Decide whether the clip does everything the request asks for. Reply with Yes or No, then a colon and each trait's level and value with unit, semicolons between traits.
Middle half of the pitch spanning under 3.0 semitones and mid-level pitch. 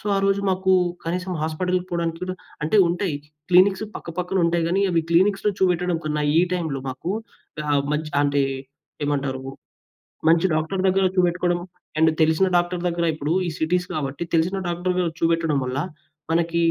Yes: narrow, 2.5 semitones; medium, 170 Hz